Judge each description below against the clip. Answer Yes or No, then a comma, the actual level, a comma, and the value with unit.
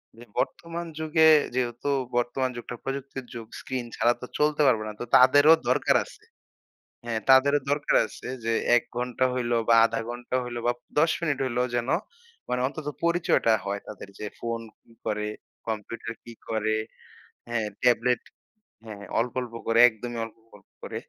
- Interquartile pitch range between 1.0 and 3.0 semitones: Yes, narrow, 2.6 semitones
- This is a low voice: Yes, low, 120 Hz